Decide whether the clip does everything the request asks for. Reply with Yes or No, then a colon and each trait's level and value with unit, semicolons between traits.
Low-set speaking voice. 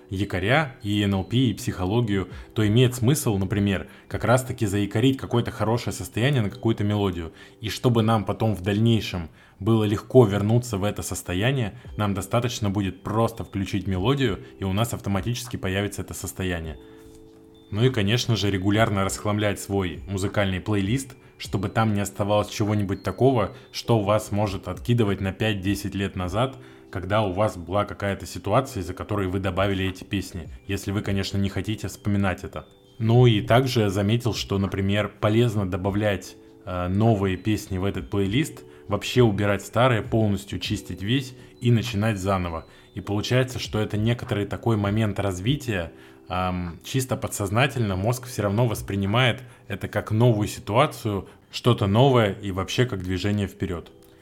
Yes: low, 105 Hz